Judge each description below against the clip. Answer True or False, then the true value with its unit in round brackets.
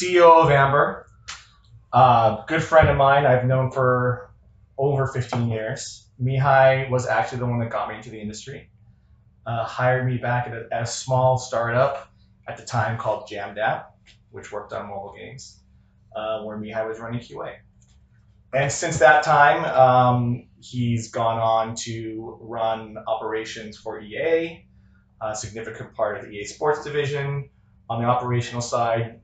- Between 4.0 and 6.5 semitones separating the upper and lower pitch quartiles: False (3.2 semitones)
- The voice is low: True (120 Hz)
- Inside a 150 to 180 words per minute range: True (160 wpm)